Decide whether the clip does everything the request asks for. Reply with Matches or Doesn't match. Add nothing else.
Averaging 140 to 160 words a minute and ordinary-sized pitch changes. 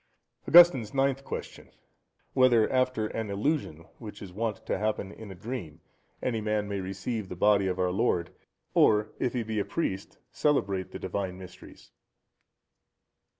Matches